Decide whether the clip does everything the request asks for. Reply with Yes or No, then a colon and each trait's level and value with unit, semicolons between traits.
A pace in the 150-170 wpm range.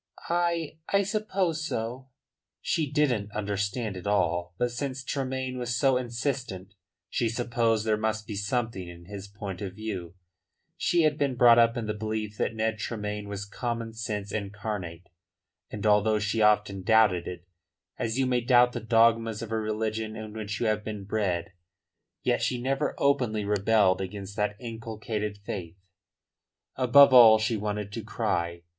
Yes: average, 160 wpm